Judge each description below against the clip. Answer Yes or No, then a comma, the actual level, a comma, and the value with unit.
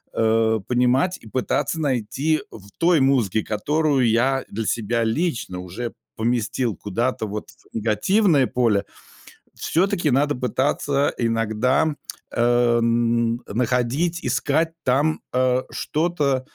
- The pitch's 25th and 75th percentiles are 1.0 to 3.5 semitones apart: No, average, 4.2 semitones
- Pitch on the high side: No, low, 125 Hz